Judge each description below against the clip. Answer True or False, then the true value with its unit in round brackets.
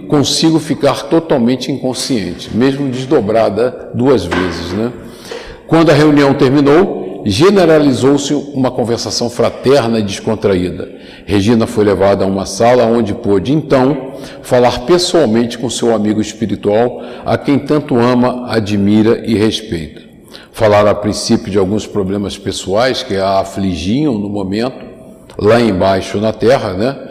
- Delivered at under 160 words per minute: True (130 wpm)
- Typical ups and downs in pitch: True (4.8 semitones)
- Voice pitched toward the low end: True (115 Hz)